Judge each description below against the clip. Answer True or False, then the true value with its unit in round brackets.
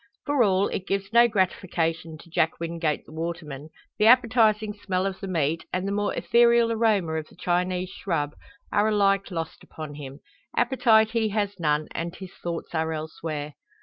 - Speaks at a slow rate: False (175 wpm)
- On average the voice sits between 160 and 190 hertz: True (185 Hz)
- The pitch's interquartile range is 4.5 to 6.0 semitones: True (4.8 semitones)